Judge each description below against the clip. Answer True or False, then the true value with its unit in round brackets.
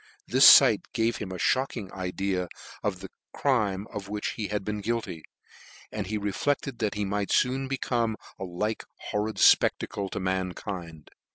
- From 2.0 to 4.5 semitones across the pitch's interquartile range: True (2.9 semitones)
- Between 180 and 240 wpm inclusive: False (160 wpm)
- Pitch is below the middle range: True (105 Hz)